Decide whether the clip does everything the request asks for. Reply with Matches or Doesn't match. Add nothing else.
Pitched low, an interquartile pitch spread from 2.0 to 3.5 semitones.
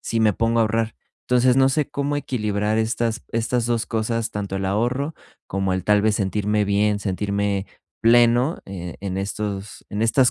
Matches